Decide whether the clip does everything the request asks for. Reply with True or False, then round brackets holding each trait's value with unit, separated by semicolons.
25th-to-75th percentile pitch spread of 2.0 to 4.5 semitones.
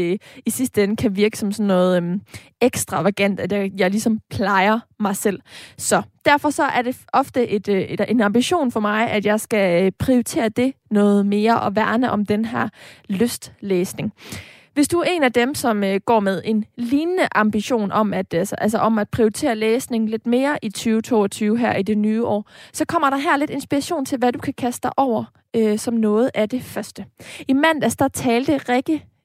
True (3.7 semitones)